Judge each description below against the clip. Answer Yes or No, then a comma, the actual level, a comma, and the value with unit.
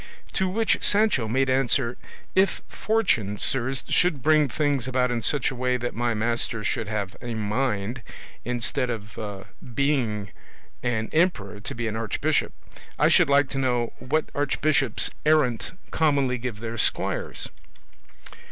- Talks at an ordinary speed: Yes, average, 145 wpm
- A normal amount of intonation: Yes, average, 3.9 semitones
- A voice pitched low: Yes, low, 125 Hz